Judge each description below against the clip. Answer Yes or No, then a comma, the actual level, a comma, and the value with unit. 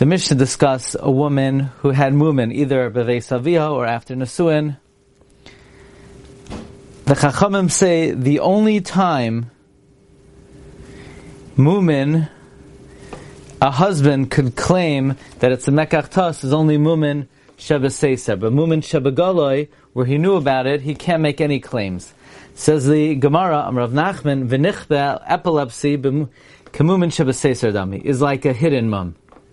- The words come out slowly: Yes, slow, 130 wpm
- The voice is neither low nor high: Yes, medium, 145 Hz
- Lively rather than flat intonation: No, average, 3.0 semitones